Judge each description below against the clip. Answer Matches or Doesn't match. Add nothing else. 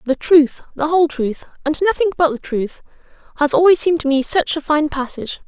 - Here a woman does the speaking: Matches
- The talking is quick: Matches